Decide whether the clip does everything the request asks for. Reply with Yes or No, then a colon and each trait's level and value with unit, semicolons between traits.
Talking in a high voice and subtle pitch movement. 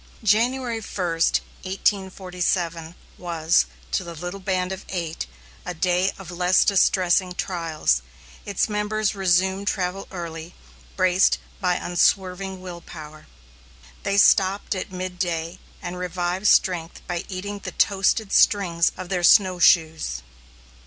No: medium, 180 Hz; narrow, 2.0 semitones